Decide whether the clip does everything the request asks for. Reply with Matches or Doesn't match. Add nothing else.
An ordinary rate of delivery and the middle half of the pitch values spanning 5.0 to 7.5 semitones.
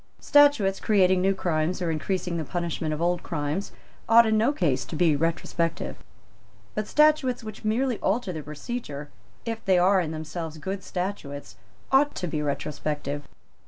Matches